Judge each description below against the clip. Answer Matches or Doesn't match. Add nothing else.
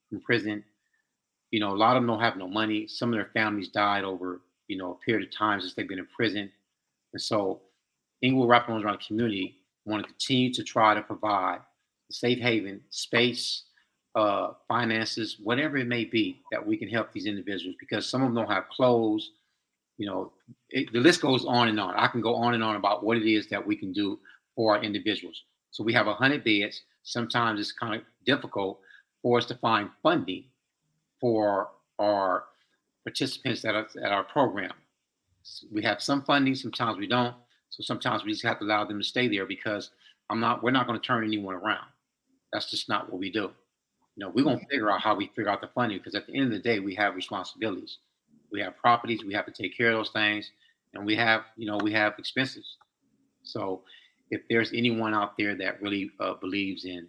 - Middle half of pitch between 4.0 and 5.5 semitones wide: Doesn't match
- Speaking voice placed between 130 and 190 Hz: Doesn't match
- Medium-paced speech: Doesn't match